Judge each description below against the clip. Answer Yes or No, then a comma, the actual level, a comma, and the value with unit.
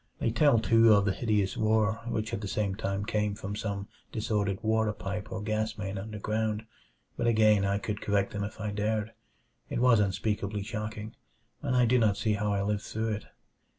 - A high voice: No, low, 105 Hz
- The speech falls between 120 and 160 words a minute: No, average, 195 wpm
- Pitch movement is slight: Yes, narrow, 1.5 semitones